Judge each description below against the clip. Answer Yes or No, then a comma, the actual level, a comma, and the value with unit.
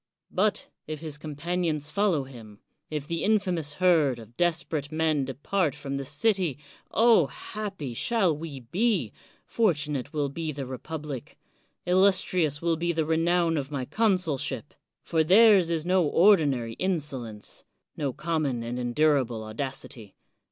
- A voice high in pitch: No, medium, 155 Hz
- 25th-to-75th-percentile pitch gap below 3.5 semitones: No, average, 4.4 semitones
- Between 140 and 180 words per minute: Yes, average, 145 wpm